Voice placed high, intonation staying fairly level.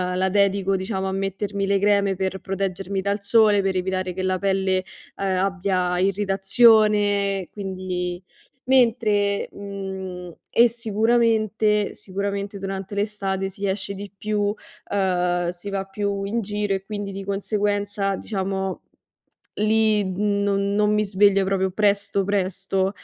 Yes: high, 195 Hz; narrow, 1.3 semitones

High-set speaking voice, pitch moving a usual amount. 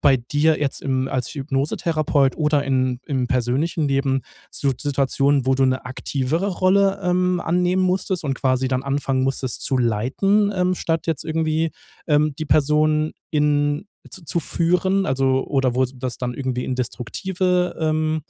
No: medium, 145 Hz; average, 4.0 semitones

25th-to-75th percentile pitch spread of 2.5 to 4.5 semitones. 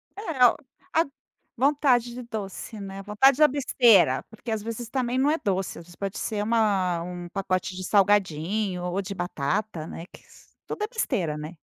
No: average, 5.0 semitones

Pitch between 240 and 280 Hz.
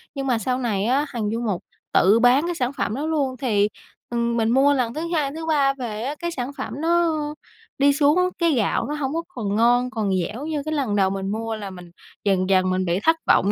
Yes: high, 245 Hz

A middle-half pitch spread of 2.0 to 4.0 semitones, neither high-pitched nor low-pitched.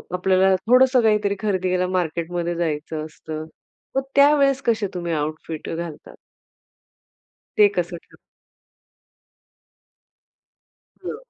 No: average, 4.5 semitones; medium, 180 Hz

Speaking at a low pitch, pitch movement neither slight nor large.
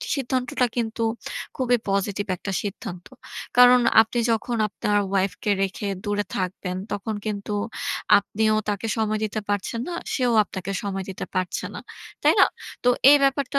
No: high, 210 Hz; average, 3.4 semitones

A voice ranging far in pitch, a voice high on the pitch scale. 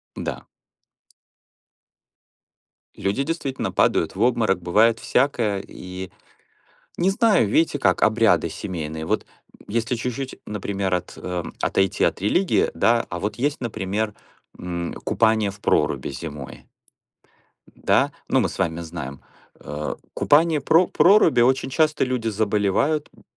No: wide, 6.2 semitones; low, 110 Hz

